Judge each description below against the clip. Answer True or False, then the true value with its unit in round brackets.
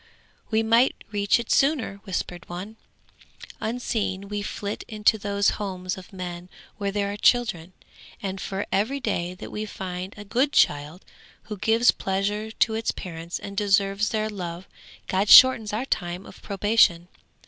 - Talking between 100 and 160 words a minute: True (155 wpm)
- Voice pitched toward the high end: True (200 Hz)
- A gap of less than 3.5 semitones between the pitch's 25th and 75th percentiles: True (2.9 semitones)